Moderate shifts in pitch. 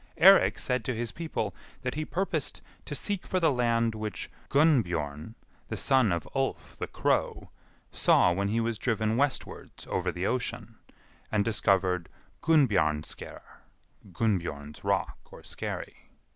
No: wide, 6.4 semitones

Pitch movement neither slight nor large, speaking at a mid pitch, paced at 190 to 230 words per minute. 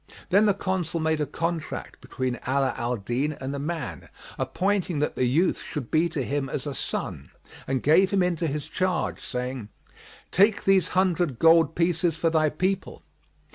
No: average, 4.6 semitones; medium, 160 Hz; average, 175 wpm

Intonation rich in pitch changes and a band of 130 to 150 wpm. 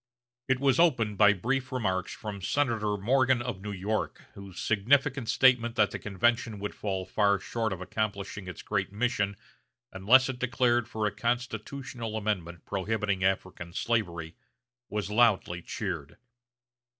No: average, 3.8 semitones; average, 140 wpm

